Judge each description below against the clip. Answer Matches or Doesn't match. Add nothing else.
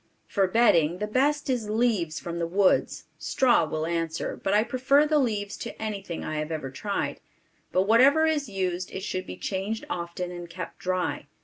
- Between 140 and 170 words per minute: Doesn't match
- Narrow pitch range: Doesn't match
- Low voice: Doesn't match